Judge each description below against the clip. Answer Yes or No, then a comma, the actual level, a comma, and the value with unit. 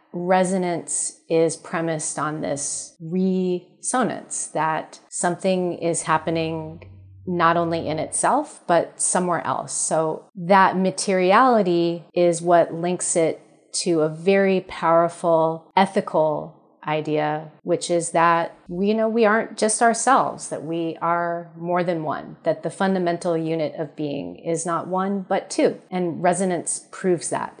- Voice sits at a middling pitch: Yes, medium, 170 Hz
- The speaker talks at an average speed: No, slow, 130 wpm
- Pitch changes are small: Yes, narrow, 2.3 semitones